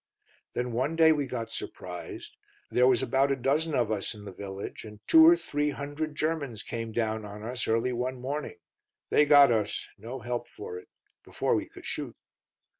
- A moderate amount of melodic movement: Yes, average, 4.6 semitones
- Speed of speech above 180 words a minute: Yes, average, 190 wpm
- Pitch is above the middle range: No, low, 125 Hz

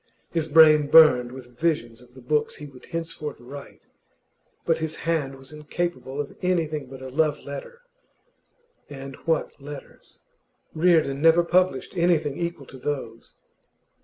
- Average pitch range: Yes, average, 3.4 semitones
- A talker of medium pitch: Yes, medium, 150 Hz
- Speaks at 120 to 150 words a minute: Yes, average, 140 wpm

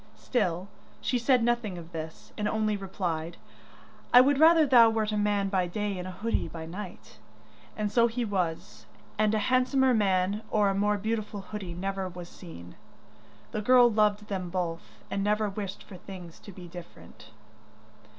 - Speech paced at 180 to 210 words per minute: No, average, 170 wpm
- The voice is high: Yes, high, 205 Hz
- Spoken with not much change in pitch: No, average, 3.3 semitones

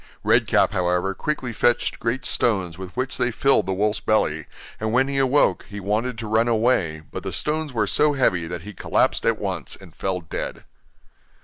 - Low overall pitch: Yes, low, 110 Hz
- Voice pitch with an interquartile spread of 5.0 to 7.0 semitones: Yes, average, 5.3 semitones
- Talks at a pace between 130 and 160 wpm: No, average, 195 wpm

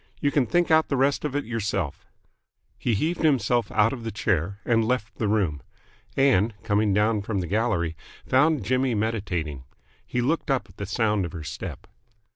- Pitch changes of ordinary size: Yes, average, 4.7 semitones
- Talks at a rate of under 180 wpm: No, average, 185 wpm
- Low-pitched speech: Yes, low, 110 Hz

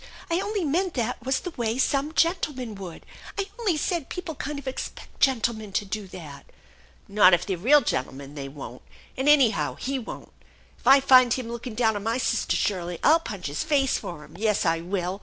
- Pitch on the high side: Yes, high, 235 Hz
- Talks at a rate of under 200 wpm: No, fast, 205 wpm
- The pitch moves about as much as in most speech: No, wide, 7.4 semitones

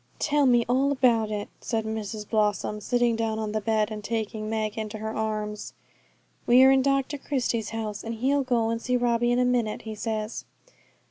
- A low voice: No, high, 225 Hz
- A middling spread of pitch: No, narrow, 2.3 semitones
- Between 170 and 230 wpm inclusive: Yes, average, 190 wpm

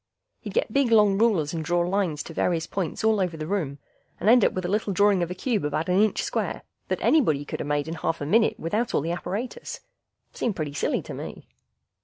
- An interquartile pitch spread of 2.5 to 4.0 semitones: No, average, 4.8 semitones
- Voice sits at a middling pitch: Yes, medium, 180 Hz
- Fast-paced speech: Yes, fast, 235 wpm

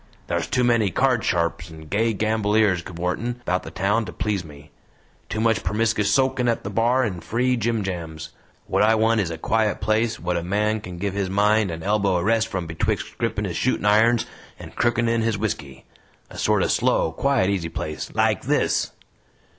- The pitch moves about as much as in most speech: Yes, average, 4.3 semitones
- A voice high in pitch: No, low, 105 Hz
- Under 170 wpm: No, average, 195 wpm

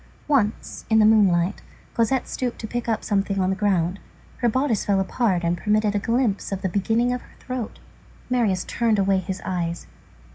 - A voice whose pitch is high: Yes, high, 210 Hz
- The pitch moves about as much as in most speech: Yes, average, 3.6 semitones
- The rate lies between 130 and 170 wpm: No, average, 185 wpm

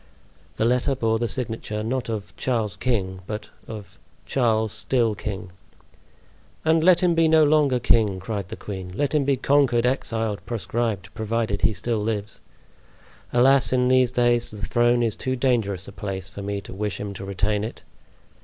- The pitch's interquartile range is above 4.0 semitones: No, average, 3.6 semitones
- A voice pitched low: Yes, low, 115 Hz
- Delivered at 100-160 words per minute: No, average, 170 wpm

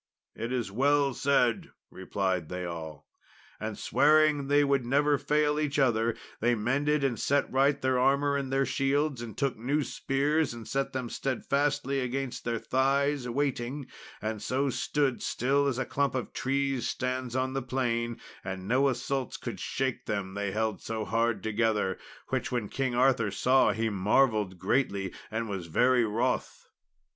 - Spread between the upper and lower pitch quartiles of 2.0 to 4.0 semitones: Yes, average, 3.5 semitones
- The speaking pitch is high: No, low, 130 Hz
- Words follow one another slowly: No, average, 160 wpm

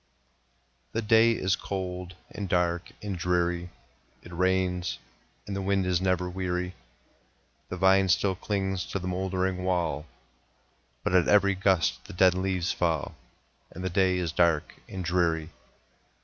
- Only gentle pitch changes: Yes, narrow, 1.4 semitones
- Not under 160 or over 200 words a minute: No, average, 145 wpm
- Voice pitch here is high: No, very low, 90 Hz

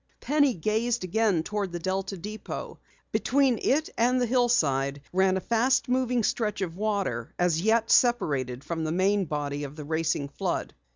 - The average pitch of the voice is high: Yes, high, 195 Hz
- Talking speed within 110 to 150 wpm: No, average, 160 wpm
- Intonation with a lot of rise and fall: Yes, wide, 6.7 semitones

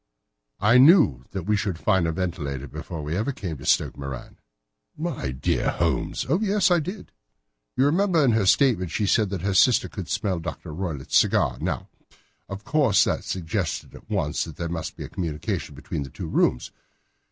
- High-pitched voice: No, very low, 95 Hz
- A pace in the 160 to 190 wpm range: Yes, average, 185 wpm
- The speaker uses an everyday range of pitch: No, wide, 7.9 semitones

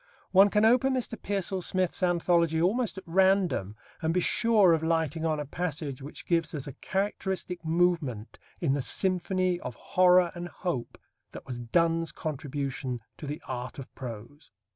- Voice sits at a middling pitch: Yes, medium, 170 Hz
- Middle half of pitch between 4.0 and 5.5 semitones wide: Yes, average, 4.4 semitones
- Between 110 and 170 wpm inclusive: Yes, average, 165 wpm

